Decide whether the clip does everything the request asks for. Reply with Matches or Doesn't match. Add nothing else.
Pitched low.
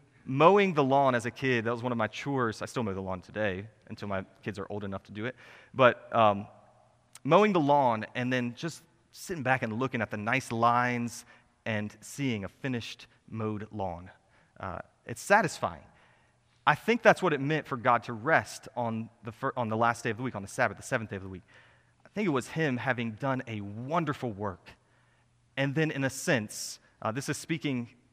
Matches